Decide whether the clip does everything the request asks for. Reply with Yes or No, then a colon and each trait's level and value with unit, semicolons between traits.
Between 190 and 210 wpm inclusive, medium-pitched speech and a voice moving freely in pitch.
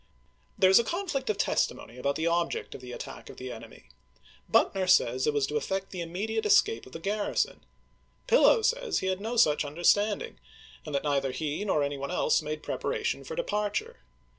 Yes: fast, 205 wpm; medium, 175 Hz; wide, 6.8 semitones